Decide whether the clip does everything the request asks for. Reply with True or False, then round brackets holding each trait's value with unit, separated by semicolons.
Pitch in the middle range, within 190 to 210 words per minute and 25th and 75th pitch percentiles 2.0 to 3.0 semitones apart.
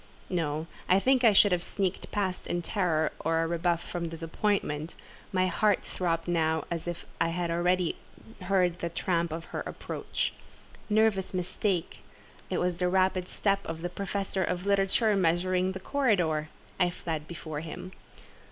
False (180 Hz; 155 wpm; 2.6 semitones)